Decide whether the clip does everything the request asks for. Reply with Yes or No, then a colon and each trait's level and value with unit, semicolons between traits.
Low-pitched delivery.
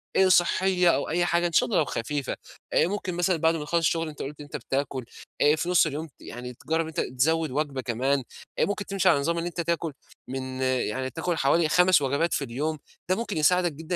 No: medium, 160 Hz